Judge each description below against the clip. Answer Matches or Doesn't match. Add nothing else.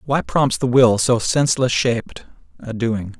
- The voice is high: Doesn't match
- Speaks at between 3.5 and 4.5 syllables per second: Matches